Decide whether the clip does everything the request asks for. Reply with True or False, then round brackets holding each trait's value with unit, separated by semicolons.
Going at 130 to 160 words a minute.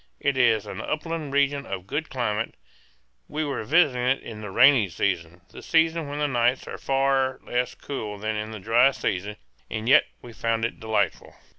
False (185 wpm)